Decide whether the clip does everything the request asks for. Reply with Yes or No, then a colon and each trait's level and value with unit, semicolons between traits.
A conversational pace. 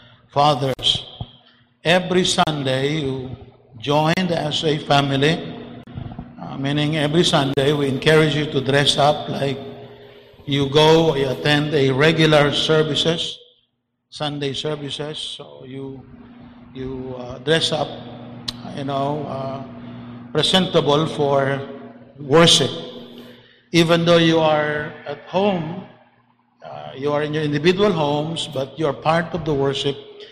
No: slow, 120 wpm